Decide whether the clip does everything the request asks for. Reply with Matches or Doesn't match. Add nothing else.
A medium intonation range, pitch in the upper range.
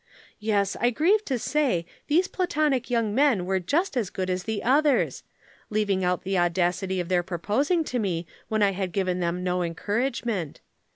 Doesn't match